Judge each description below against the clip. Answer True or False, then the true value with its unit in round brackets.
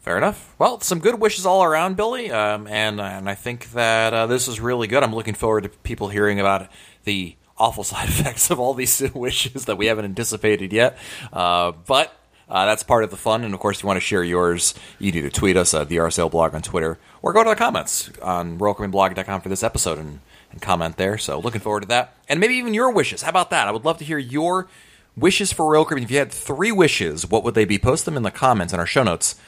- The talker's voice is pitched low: True (110 Hz)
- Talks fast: True (250 wpm)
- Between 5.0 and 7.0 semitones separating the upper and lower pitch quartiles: True (5.6 semitones)